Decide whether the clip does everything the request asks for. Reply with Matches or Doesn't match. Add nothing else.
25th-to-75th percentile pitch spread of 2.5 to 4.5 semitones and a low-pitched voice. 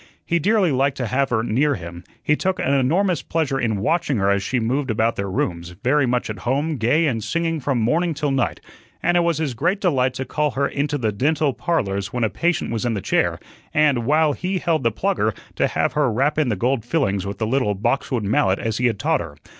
Doesn't match